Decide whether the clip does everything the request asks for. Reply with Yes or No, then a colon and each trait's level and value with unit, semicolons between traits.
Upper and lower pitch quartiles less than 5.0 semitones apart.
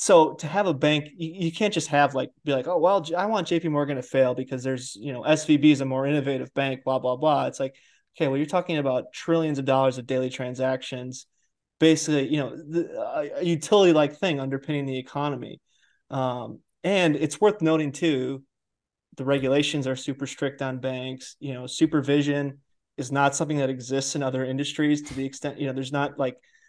Yes: average, 2.8 semitones